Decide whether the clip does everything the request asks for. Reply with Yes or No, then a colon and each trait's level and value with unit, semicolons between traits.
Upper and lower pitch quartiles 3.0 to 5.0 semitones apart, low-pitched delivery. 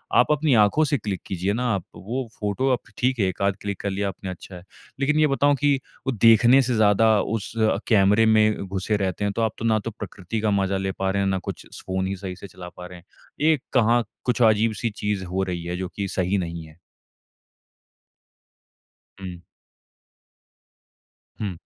Yes: average, 3.4 semitones; low, 100 Hz